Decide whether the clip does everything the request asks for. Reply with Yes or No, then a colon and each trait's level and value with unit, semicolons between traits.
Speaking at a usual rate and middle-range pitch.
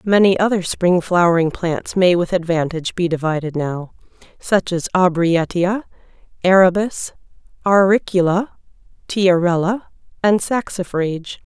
No: slow, 100 wpm; medium, 180 Hz